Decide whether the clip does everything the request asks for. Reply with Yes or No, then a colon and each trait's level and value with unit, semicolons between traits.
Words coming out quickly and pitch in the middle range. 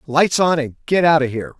Yes: fast, 265 wpm; medium, 150 Hz